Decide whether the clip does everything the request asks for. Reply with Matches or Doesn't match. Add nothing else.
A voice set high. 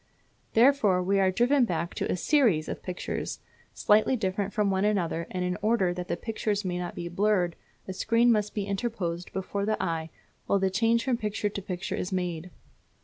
Matches